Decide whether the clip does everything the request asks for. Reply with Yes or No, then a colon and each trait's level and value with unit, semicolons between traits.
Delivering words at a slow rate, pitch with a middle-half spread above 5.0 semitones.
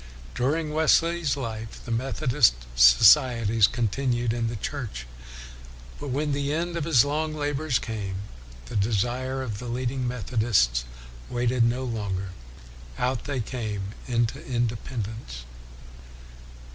No: slow, 120 wpm; average, 4.1 semitones